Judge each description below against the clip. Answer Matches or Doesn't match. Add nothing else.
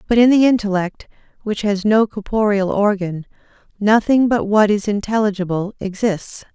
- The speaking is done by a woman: Matches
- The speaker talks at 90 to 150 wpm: Matches